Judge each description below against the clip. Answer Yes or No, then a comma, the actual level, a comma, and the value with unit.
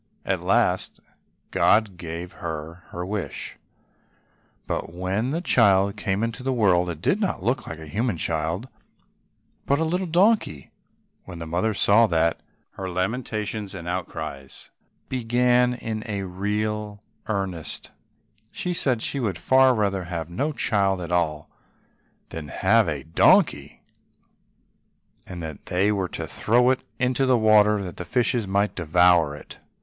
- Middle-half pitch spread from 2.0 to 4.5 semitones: No, average, 5.1 semitones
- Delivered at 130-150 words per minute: Yes, average, 145 wpm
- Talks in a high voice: No, low, 100 Hz